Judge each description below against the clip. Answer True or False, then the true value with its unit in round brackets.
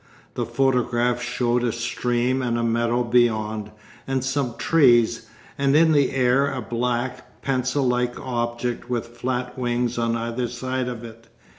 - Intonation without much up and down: True (1.5 semitones)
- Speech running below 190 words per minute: True (150 wpm)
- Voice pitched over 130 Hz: False (125 Hz)